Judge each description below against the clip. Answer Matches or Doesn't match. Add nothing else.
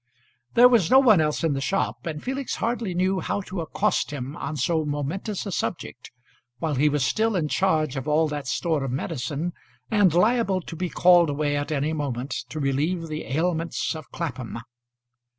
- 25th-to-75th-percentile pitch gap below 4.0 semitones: Doesn't match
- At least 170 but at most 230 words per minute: Matches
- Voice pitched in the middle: Matches